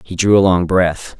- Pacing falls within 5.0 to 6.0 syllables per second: No, 4.6 syllables/s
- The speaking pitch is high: No, very low, 90 Hz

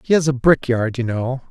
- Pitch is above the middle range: No, low, 130 Hz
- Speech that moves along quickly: Yes, fast, 280 wpm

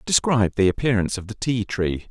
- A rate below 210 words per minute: Yes, average, 200 wpm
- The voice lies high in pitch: No, low, 110 Hz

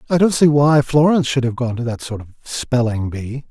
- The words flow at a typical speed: No, fast, 240 wpm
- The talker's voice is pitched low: Yes, low, 130 Hz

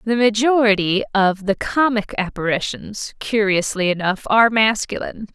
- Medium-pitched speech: No, high, 210 Hz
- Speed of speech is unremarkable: No, slow, 110 wpm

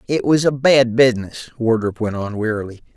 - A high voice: No, low, 120 Hz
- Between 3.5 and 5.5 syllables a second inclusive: No, 5.7 syllables/s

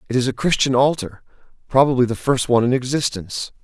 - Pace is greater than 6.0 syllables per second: Yes, 6.6 syllables/s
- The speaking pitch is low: Yes, low, 125 Hz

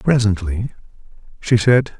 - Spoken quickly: No, slow, 90 wpm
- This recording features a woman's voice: No, male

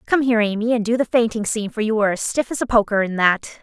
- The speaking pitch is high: Yes, high, 220 Hz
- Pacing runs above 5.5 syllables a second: Yes, 6.9 syllables/s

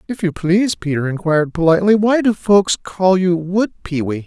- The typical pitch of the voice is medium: Yes, medium, 180 Hz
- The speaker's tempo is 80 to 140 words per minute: No, average, 185 wpm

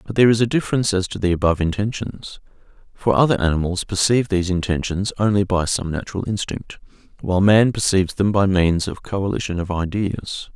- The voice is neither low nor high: No, very low, 95 Hz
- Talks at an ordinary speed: Yes, average, 175 wpm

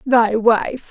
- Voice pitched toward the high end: Yes, high, 230 Hz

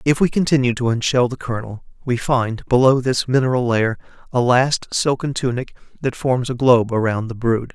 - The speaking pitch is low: Yes, low, 125 Hz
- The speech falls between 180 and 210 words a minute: Yes, average, 185 wpm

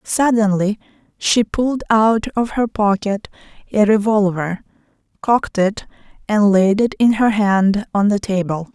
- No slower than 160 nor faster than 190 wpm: No, slow, 135 wpm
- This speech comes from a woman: Yes, female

